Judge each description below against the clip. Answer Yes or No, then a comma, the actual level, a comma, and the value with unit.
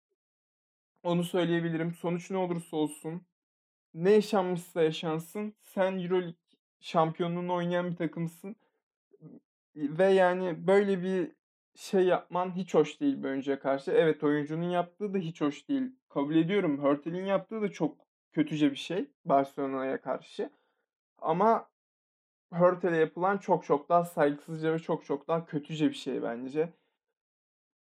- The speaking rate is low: No, average, 125 wpm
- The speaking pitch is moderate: Yes, medium, 175 Hz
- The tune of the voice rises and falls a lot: No, average, 3.2 semitones